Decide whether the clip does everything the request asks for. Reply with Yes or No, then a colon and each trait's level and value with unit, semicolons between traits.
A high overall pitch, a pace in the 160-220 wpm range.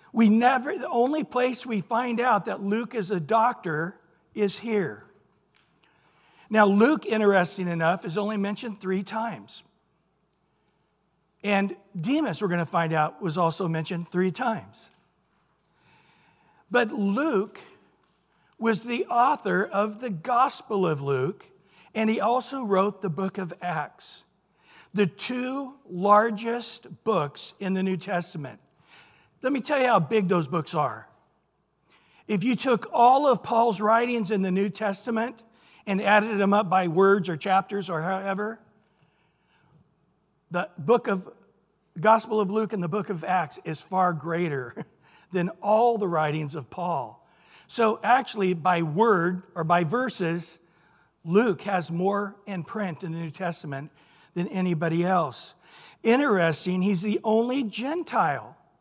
No: high, 200 Hz; average, 140 wpm